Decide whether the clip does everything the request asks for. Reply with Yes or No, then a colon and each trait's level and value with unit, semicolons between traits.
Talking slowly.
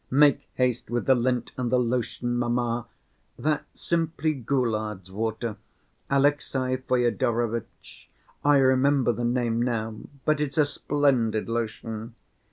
Yes: slow, 120 wpm